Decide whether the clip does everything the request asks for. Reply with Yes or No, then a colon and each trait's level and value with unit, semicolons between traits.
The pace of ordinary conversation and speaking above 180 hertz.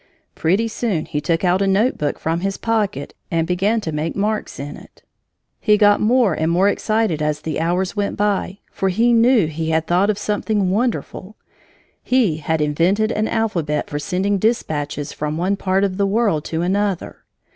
Yes: average, 180 wpm; high, 190 Hz